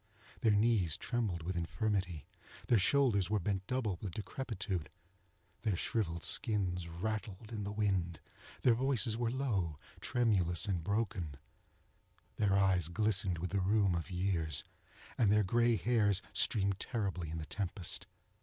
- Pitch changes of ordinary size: Yes, average, 3.7 semitones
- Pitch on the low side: Yes, low, 100 Hz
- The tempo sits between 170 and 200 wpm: No, average, 140 wpm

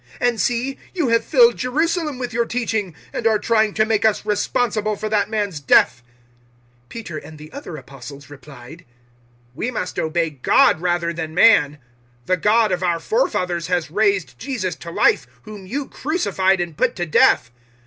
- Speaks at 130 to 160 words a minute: No, average, 175 wpm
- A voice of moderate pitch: No, high, 200 Hz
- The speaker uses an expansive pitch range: Yes, wide, 5.8 semitones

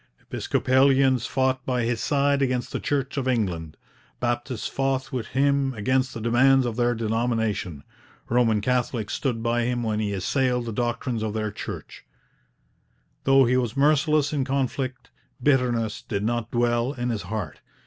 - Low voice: Yes, low, 120 Hz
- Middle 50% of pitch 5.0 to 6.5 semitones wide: No, average, 2.8 semitones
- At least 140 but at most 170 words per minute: Yes, average, 155 wpm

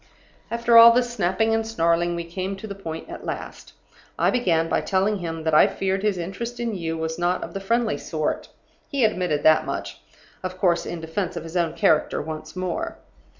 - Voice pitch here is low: No, medium, 185 Hz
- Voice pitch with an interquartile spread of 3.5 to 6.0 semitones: Yes, average, 4.7 semitones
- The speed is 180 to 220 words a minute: Yes, average, 200 wpm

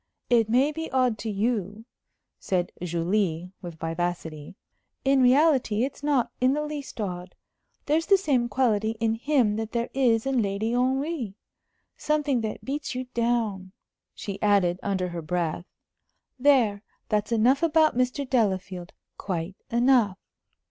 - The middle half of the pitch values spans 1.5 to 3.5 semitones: No, wide, 5.5 semitones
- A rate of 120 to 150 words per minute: Yes, average, 140 wpm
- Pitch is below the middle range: No, high, 225 Hz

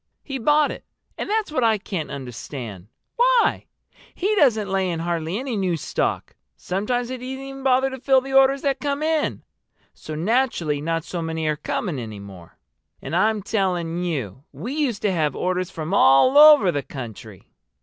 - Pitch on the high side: Yes, high, 195 Hz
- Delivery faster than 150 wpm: Yes, average, 180 wpm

